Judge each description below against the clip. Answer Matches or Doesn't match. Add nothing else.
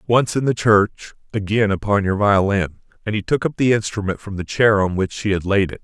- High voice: Doesn't match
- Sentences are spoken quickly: Matches